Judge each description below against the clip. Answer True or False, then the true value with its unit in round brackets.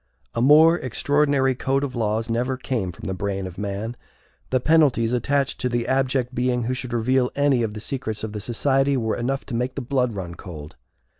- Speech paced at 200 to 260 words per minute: True (205 wpm)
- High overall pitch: False (125 Hz)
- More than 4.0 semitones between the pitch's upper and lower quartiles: False (3.3 semitones)